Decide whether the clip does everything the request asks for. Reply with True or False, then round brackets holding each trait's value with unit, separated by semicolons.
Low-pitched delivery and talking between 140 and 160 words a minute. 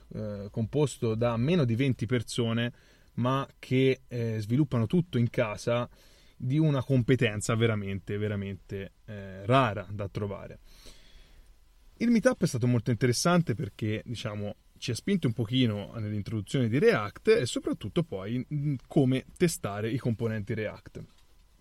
False (120 Hz; 120 wpm)